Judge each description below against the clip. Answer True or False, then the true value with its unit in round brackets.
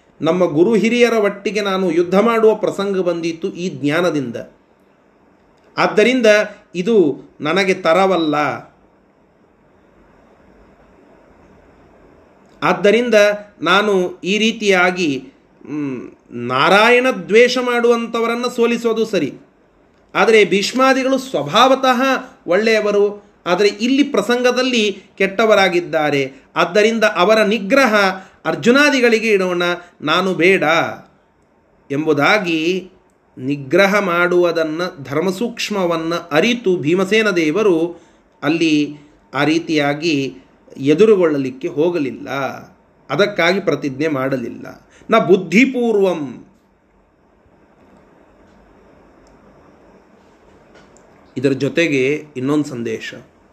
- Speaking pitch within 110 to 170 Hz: False (190 Hz)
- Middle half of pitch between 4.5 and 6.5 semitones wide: True (5.1 semitones)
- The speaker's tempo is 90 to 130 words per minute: False (65 wpm)